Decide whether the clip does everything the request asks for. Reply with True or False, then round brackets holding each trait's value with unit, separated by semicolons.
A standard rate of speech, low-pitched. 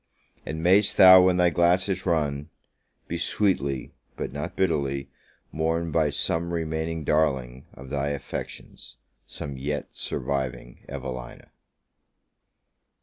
False (115 wpm; 80 Hz)